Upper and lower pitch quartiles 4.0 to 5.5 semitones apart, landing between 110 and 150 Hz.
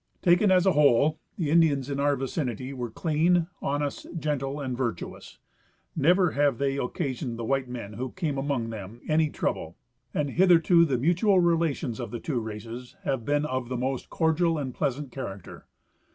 Yes: average, 4.4 semitones; medium, 140 Hz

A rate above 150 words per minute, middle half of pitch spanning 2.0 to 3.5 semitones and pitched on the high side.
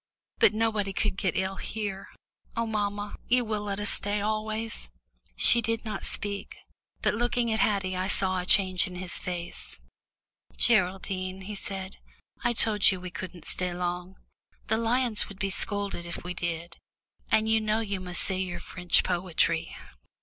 Yes: average, 165 wpm; average, 2.8 semitones; high, 195 Hz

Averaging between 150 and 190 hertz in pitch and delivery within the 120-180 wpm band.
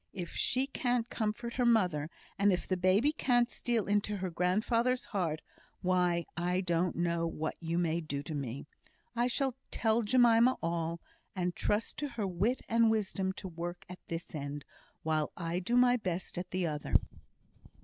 Yes: medium, 185 Hz; average, 170 wpm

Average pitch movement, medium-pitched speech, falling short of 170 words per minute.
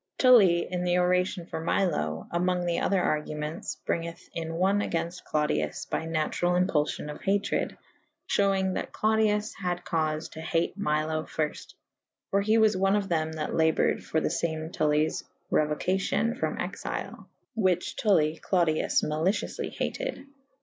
Yes: average, 3.6 semitones; medium, 170 Hz; average, 155 wpm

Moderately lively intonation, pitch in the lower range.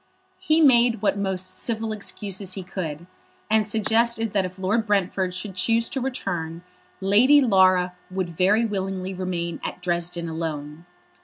No: average, 3.5 semitones; high, 190 Hz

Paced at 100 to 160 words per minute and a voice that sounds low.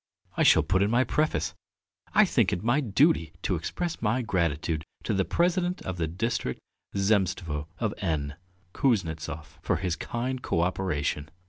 Yes: average, 155 wpm; very low, 95 Hz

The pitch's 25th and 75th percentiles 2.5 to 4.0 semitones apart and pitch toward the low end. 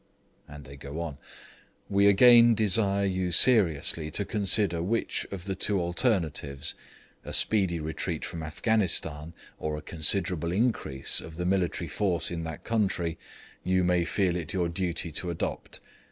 Yes: average, 3.6 semitones; very low, 90 Hz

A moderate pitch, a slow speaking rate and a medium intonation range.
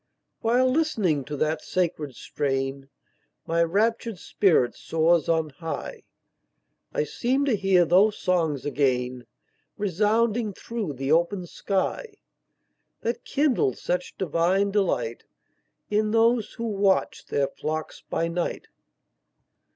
No: medium, 180 Hz; slow, 110 wpm; wide, 6.0 semitones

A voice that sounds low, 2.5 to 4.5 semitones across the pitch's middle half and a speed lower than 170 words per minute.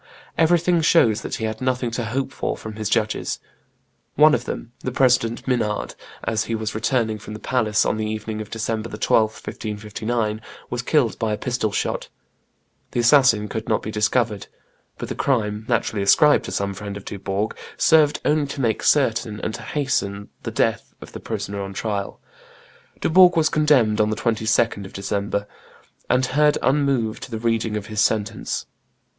No: low, 110 Hz; average, 3.2 semitones; average, 175 wpm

